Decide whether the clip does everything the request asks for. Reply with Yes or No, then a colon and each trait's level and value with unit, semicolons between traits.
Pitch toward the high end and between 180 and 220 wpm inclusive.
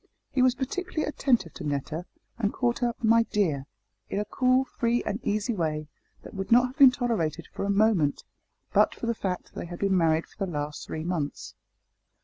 Yes: high, 205 Hz; average, 200 wpm